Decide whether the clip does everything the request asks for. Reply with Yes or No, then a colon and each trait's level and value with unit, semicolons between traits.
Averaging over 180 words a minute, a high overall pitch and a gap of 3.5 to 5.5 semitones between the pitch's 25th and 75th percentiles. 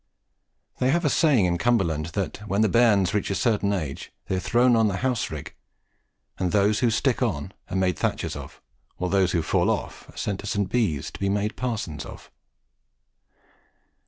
No: average, 200 wpm; low, 100 Hz; average, 4.1 semitones